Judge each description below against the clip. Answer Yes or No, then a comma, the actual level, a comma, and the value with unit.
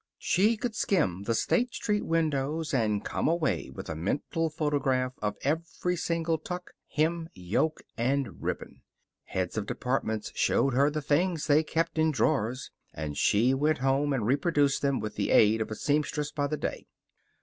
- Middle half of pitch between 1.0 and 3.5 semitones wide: No, average, 4.8 semitones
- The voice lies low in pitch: No, medium, 145 Hz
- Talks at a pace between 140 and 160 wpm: No, average, 170 wpm